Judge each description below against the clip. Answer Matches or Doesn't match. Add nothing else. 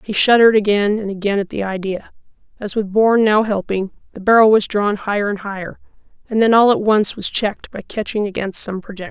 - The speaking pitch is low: Doesn't match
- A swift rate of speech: Matches